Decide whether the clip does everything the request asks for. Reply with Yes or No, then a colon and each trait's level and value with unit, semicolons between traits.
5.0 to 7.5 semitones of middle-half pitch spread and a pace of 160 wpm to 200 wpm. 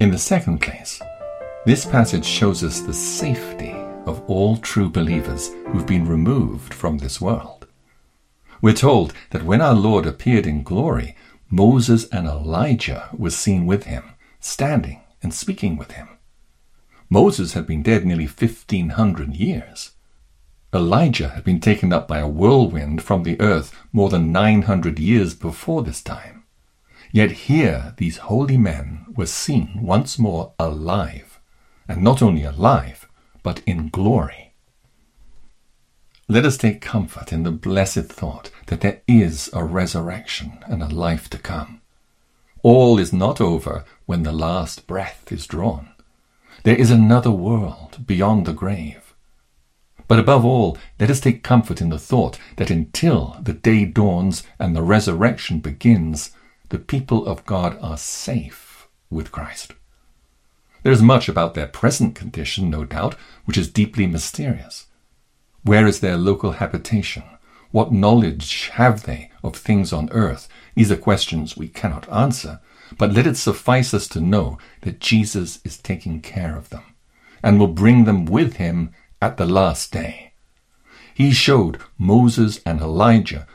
No: wide, 5.5 semitones; average, 150 wpm